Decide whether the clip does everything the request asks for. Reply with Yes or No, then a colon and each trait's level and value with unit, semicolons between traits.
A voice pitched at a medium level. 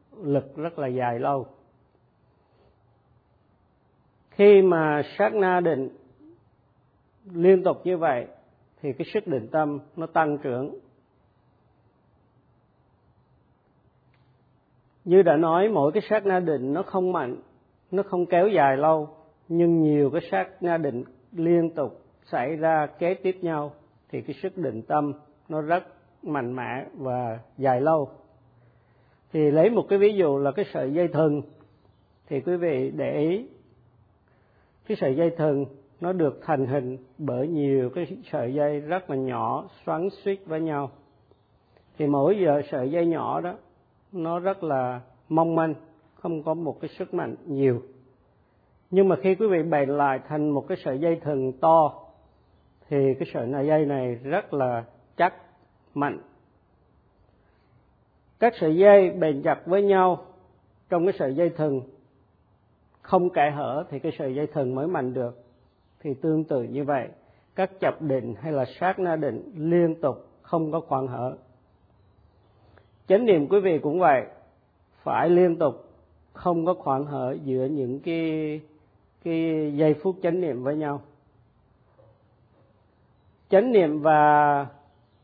Yes: medium, 150 Hz